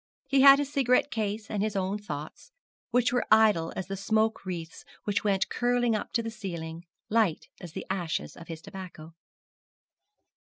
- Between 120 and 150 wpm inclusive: No, average, 170 wpm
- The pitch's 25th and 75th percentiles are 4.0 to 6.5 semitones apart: Yes, average, 4.6 semitones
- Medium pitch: No, high, 205 Hz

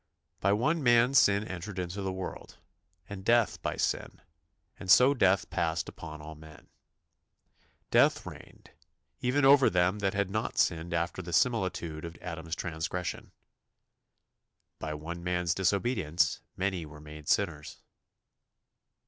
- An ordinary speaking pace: No, slow, 130 wpm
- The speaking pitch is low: Yes, very low, 90 Hz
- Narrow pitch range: No, average, 3.8 semitones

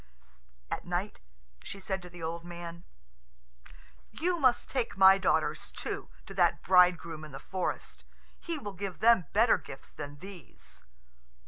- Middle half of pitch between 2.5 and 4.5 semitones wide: Yes, average, 3.1 semitones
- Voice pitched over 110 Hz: Yes, medium, 185 Hz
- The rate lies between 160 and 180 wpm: No, average, 145 wpm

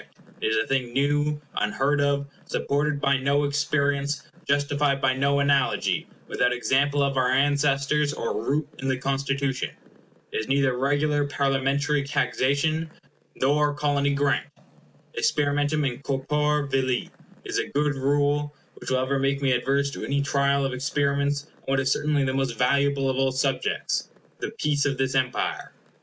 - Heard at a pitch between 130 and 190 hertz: Yes, medium, 140 Hz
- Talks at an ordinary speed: Yes, average, 155 wpm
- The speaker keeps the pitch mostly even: Yes, narrow, 1.3 semitones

